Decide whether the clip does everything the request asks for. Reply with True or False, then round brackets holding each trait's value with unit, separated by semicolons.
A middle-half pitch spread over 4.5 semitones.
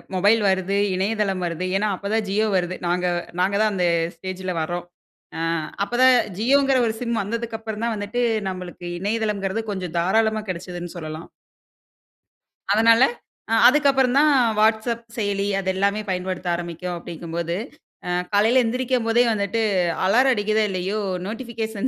False (3.7 semitones)